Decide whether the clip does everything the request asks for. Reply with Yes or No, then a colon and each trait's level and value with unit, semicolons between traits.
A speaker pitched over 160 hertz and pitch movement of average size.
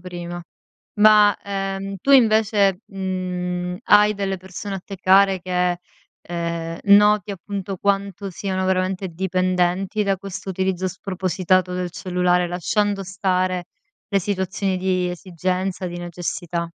No: medium, 185 Hz; narrow, 1.7 semitones